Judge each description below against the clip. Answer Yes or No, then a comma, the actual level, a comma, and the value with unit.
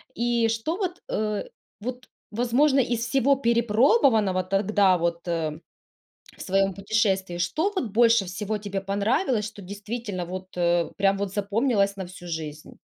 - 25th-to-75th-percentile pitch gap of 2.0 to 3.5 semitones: No, average, 3.9 semitones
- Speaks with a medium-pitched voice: No, high, 205 Hz